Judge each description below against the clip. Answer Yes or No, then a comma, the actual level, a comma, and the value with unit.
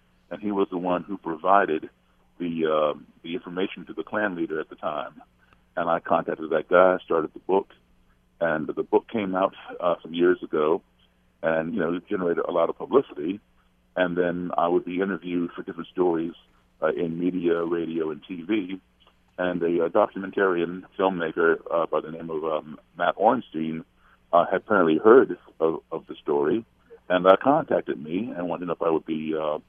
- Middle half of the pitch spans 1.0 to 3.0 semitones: Yes, average, 2.7 semitones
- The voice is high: No, very low, 85 Hz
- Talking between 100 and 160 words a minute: No, average, 185 wpm